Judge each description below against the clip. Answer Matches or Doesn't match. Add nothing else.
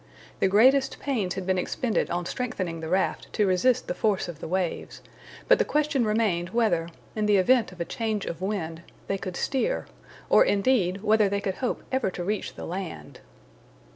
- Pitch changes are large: Doesn't match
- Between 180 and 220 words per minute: Matches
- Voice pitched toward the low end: Doesn't match